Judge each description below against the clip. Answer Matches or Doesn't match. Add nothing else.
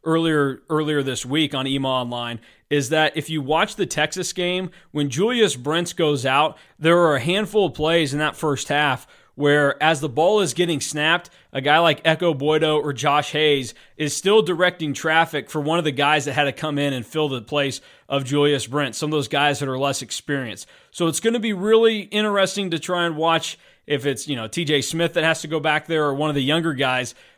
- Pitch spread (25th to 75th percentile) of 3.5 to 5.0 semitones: Doesn't match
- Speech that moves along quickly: Matches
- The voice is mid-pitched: Matches